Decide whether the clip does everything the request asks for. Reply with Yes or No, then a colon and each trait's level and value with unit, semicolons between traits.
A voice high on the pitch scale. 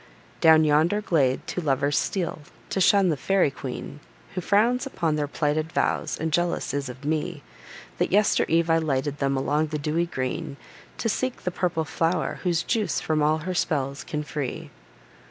No: medium, 155 Hz